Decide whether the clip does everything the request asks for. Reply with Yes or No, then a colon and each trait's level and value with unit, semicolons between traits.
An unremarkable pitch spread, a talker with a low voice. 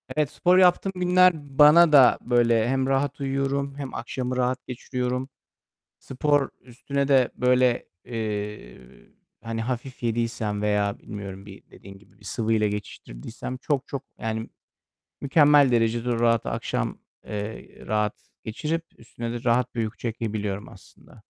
Yes: average, 3.7 semitones; low, 125 Hz